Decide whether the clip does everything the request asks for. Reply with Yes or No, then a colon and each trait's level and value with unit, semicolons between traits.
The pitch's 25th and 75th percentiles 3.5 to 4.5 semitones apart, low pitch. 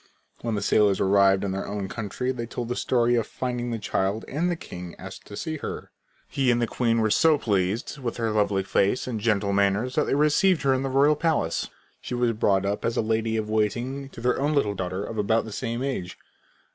Yes: average, 4.2 semitones; low, 115 Hz